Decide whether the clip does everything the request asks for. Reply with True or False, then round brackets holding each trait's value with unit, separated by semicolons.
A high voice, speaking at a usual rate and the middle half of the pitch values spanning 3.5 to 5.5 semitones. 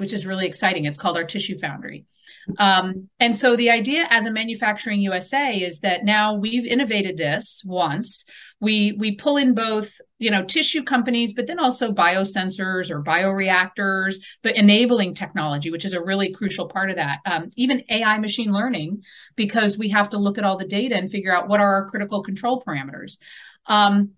False (205 Hz; 185 wpm; 3.0 semitones)